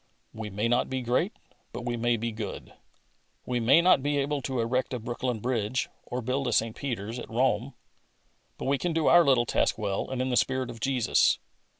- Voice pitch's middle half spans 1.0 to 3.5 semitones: Yes, narrow, 2.4 semitones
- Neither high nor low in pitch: No, low, 125 Hz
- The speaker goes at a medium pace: No, fast, 210 wpm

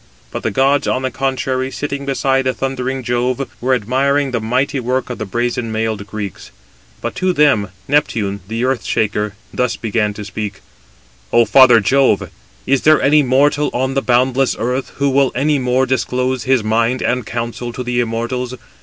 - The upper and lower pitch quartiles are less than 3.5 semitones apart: Yes, narrow, 2.6 semitones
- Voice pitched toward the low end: Yes, low, 125 Hz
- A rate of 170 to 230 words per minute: Yes, average, 175 wpm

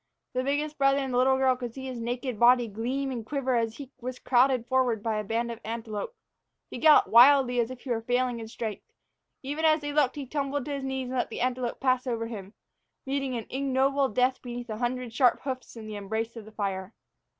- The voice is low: No, very high, 250 Hz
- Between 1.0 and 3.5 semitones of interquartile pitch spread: Yes, average, 2.7 semitones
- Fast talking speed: Yes, fast, 230 wpm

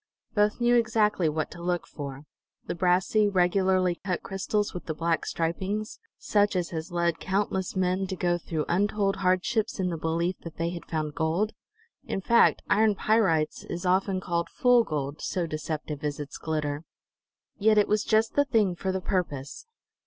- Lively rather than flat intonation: No, average, 3.7 semitones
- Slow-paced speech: No, average, 175 wpm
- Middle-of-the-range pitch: Yes, medium, 180 Hz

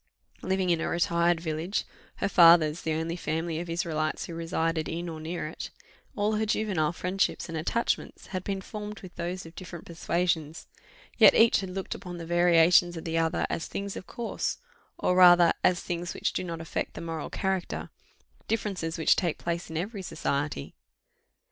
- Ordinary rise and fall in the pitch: No, narrow, 2.2 semitones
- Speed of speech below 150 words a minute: No, average, 180 wpm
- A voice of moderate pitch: Yes, medium, 170 Hz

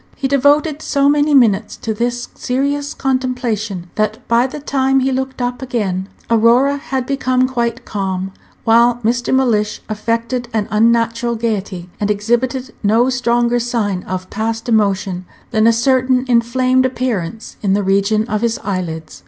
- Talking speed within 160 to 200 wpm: No, average, 150 wpm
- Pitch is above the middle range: Yes, high, 235 Hz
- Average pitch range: Yes, average, 3.4 semitones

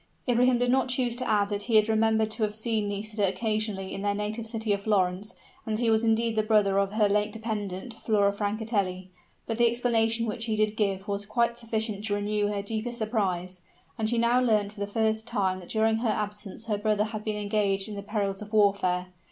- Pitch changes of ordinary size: No, narrow, 1.8 semitones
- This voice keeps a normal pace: No, fast, 220 wpm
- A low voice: No, high, 215 Hz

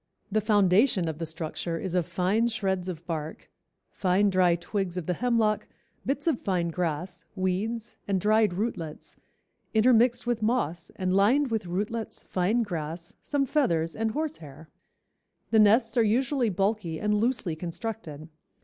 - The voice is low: No, high, 195 Hz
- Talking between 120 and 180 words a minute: Yes, average, 150 wpm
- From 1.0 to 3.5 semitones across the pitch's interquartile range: No, average, 4.7 semitones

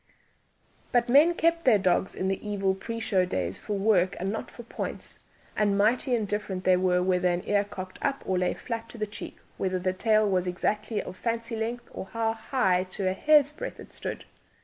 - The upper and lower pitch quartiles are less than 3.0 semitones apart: No, average, 3.6 semitones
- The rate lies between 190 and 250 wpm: Yes, fast, 205 wpm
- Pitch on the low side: No, high, 205 Hz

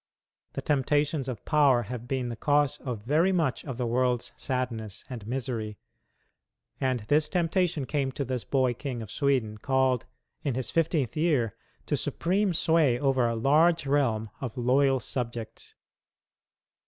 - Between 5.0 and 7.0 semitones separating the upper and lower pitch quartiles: No, average, 3.6 semitones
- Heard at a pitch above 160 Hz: No, low, 130 Hz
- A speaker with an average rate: Yes, average, 150 wpm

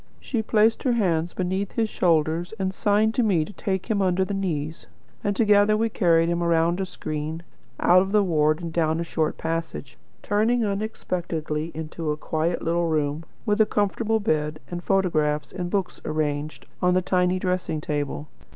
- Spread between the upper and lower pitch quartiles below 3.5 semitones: No, average, 4.2 semitones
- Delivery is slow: No, average, 180 wpm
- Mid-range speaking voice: Yes, medium, 175 Hz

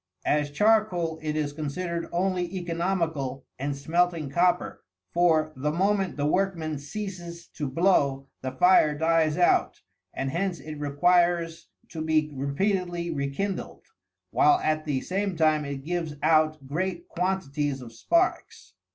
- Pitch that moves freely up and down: No, average, 3.4 semitones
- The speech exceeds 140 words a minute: No, slow, 135 wpm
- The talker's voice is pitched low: No, medium, 165 Hz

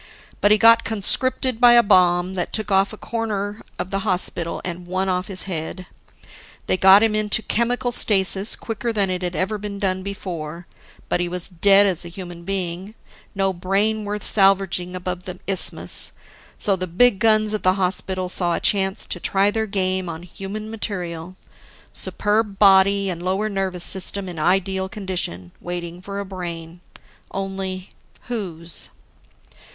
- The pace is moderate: Yes, average, 160 wpm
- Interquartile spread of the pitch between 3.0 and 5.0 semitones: No, narrow, 2.4 semitones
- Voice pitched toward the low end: No, high, 190 Hz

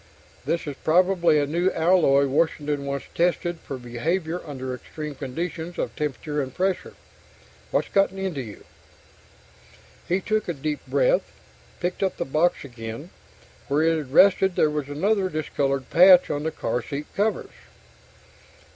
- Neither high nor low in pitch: Yes, medium, 155 Hz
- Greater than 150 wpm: No, average, 145 wpm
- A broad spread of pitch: No, average, 4.3 semitones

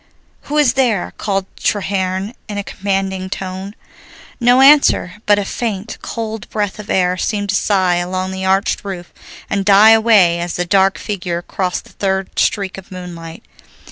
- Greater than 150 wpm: Yes, average, 165 wpm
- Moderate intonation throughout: No, narrow, 2.1 semitones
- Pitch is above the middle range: Yes, high, 195 Hz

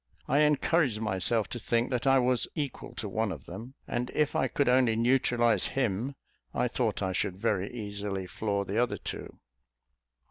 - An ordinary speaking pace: Yes, average, 175 wpm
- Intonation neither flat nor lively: Yes, average, 4.1 semitones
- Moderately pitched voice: No, low, 115 Hz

